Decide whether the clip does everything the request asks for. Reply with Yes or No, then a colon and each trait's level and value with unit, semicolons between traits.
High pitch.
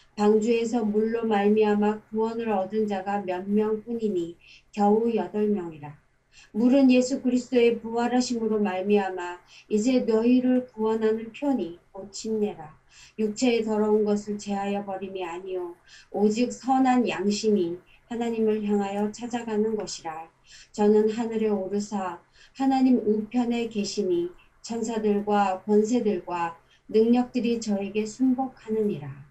Yes: high, 215 Hz